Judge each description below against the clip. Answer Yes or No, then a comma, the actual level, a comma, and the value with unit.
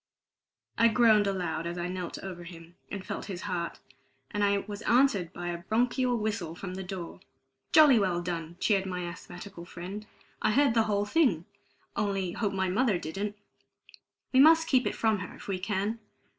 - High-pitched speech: Yes, high, 195 Hz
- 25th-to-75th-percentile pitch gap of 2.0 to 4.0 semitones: Yes, average, 3.7 semitones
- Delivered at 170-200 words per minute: Yes, average, 180 wpm